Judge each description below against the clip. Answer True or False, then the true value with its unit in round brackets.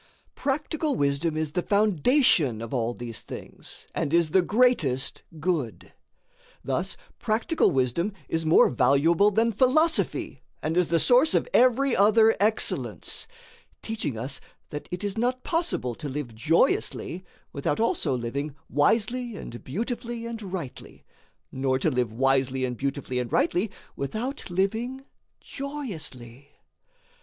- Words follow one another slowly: True (130 wpm)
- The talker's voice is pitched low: False (170 Hz)